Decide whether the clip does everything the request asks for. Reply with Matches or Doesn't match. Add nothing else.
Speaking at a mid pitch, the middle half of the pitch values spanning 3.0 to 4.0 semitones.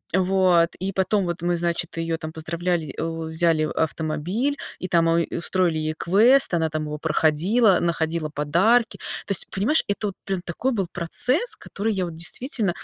Matches